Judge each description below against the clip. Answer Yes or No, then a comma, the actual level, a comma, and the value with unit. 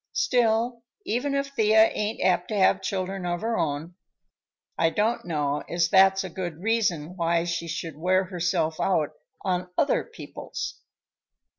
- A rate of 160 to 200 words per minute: No, average, 150 wpm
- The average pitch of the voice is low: No, medium, 185 Hz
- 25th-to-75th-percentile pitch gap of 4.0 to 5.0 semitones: Yes, average, 4.6 semitones